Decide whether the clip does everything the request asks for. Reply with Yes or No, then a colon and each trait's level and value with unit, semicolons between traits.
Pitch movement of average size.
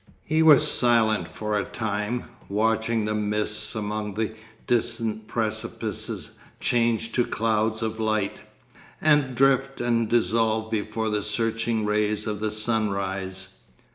No: narrow, 1.5 semitones